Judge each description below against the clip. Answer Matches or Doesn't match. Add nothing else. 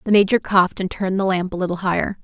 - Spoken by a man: Doesn't match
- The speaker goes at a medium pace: Doesn't match